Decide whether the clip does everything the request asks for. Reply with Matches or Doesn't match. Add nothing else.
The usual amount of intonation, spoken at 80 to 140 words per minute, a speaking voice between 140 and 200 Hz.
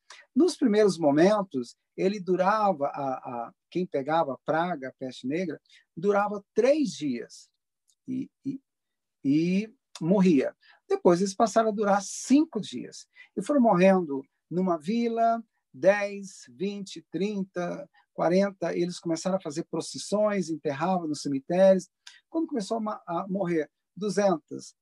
Matches